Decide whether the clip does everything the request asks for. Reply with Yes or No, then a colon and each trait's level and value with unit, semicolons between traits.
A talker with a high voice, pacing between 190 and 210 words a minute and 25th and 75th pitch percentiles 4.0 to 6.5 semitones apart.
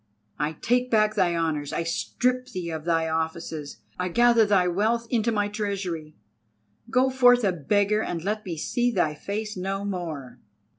No: high, 195 Hz; average, 165 wpm; average, 5.2 semitones